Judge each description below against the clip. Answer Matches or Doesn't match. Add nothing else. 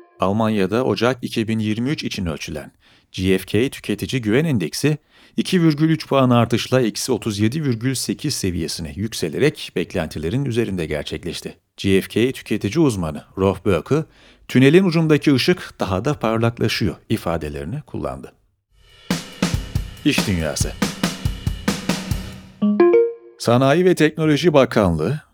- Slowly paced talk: Matches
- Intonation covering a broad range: Matches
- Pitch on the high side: Doesn't match